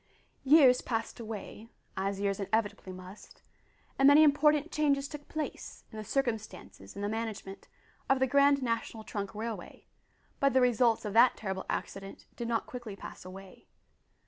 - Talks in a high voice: Yes, high, 225 Hz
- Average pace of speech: Yes, average, 155 wpm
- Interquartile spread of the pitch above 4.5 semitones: Yes, average, 5.2 semitones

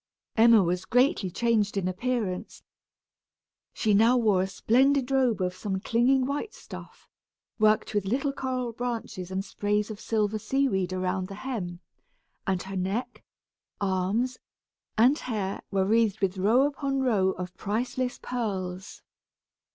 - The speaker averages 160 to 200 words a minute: No, slow, 135 wpm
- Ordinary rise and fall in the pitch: Yes, average, 4.6 semitones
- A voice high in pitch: Yes, high, 215 Hz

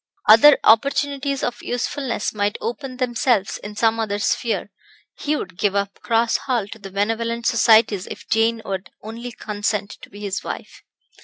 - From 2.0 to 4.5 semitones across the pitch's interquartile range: Yes, average, 2.8 semitones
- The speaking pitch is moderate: No, high, 225 Hz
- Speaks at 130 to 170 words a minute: Yes, average, 160 wpm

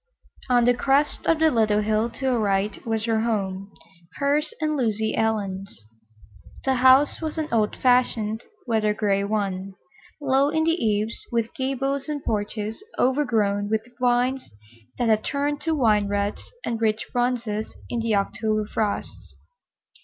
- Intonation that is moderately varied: Yes, average, 3.9 semitones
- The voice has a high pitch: Yes, high, 225 Hz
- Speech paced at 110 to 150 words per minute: Yes, average, 145 wpm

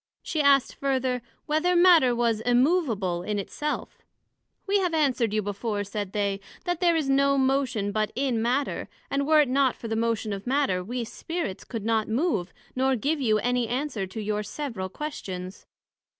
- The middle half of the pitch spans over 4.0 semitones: Yes, average, 5.0 semitones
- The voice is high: Yes, high, 245 Hz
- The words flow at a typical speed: Yes, average, 180 wpm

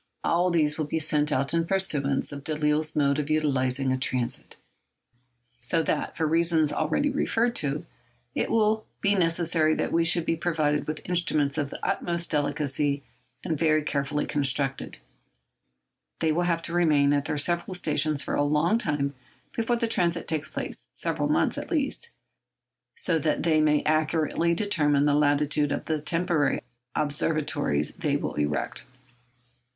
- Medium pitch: Yes, medium, 155 Hz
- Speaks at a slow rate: No, average, 155 wpm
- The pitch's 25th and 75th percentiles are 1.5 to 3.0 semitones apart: Yes, average, 2.7 semitones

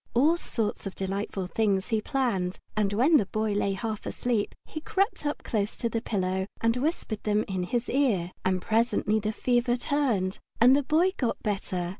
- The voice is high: Yes, high, 220 Hz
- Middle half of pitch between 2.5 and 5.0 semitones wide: Yes, average, 4.2 semitones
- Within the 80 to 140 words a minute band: No, average, 185 wpm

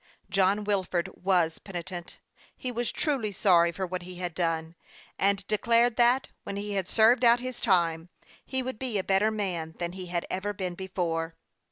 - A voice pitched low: No, high, 190 Hz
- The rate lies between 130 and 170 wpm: No, average, 180 wpm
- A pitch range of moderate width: Yes, average, 3.8 semitones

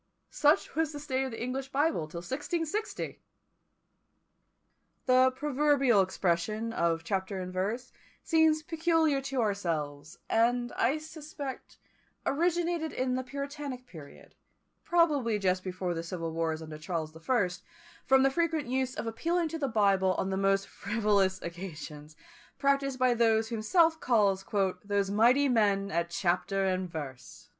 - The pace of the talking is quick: No, average, 145 wpm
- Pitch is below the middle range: No, high, 230 Hz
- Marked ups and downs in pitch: Yes, wide, 7.2 semitones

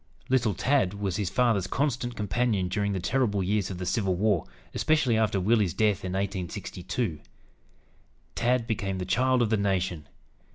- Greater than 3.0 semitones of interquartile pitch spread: Yes, average, 4.1 semitones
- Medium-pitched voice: No, low, 100 Hz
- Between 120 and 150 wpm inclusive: No, average, 160 wpm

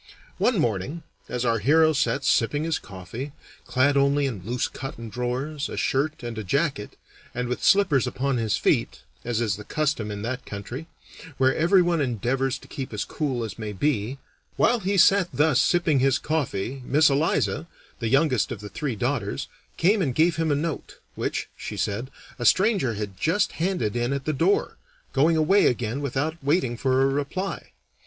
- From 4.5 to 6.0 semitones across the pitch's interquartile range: Yes, average, 5.0 semitones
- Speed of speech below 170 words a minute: No, average, 180 wpm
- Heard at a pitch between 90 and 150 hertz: Yes, low, 135 Hz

